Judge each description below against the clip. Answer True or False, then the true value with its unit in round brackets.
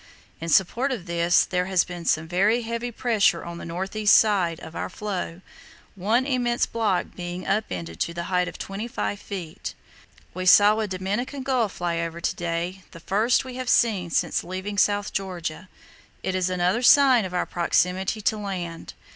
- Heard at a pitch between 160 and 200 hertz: True (190 Hz)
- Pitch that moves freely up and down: False (3.9 semitones)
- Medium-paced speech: True (180 wpm)